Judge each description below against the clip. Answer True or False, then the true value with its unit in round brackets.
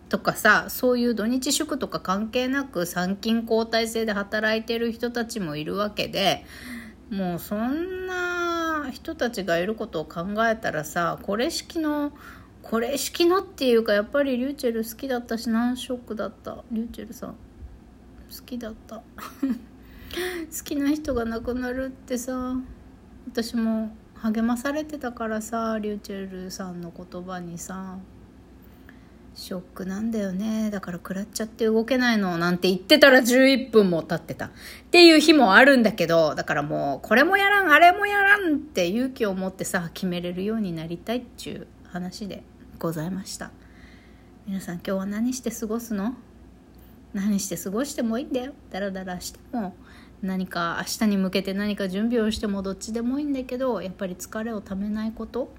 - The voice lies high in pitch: True (225 Hz)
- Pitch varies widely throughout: False (4.9 semitones)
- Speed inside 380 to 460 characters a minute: False (335 characters per minute)